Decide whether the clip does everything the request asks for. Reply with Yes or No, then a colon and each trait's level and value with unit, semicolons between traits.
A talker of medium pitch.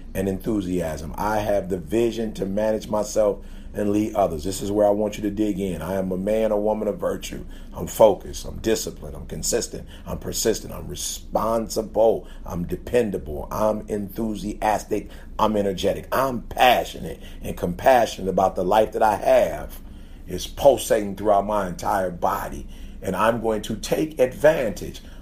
No: low, 100 Hz